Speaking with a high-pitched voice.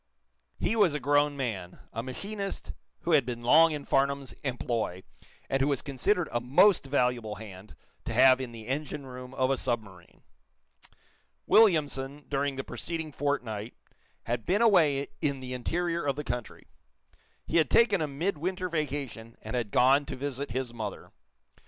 No: low, 135 Hz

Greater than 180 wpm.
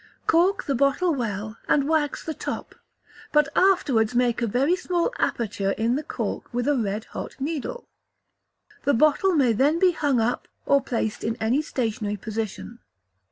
No: average, 160 wpm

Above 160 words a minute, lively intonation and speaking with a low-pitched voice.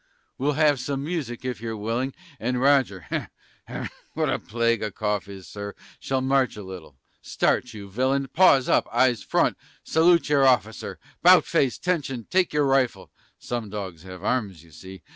No: average, 170 wpm; average, 4.9 semitones; low, 125 Hz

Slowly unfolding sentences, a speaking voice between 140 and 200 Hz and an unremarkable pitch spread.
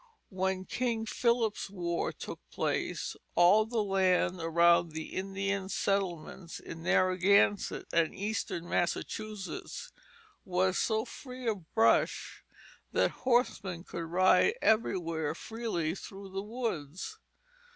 Yes: slow, 110 wpm; high, 190 Hz; average, 3.9 semitones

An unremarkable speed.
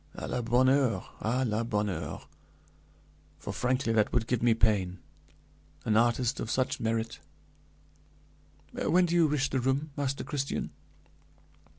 Yes: average, 145 wpm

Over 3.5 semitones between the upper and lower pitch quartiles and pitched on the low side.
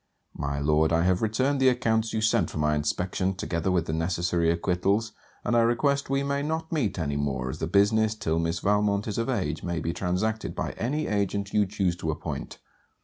Yes: average, 5.2 semitones; very low, 95 Hz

